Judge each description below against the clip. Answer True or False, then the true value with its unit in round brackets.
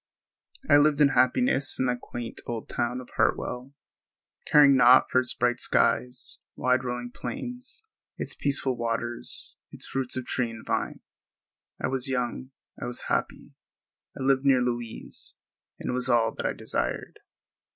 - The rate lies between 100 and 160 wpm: True (150 wpm)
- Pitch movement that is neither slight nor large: False (1.7 semitones)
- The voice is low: True (125 Hz)